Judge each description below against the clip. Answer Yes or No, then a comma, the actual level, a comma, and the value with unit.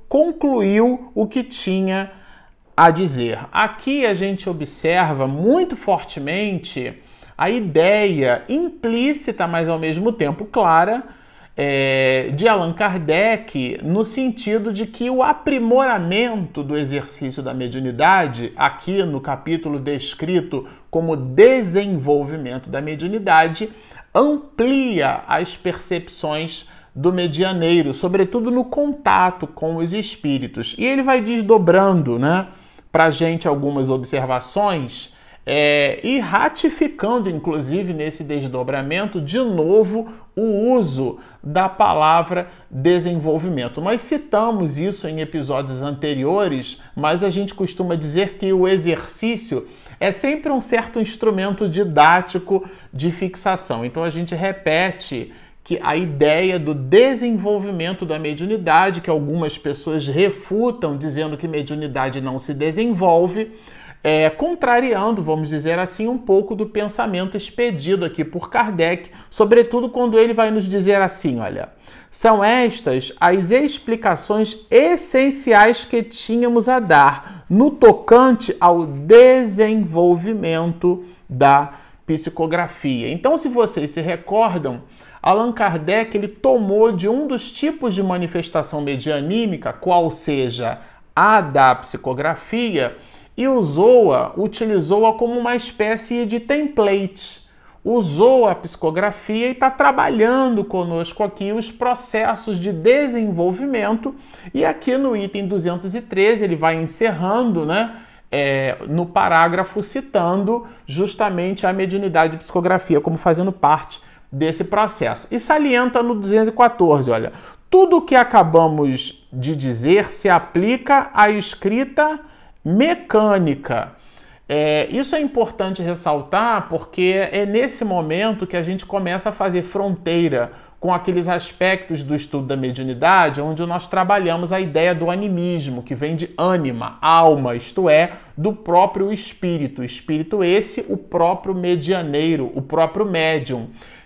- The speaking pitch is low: No, medium, 185 Hz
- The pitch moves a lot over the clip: Yes, wide, 6.0 semitones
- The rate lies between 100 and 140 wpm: Yes, slow, 120 wpm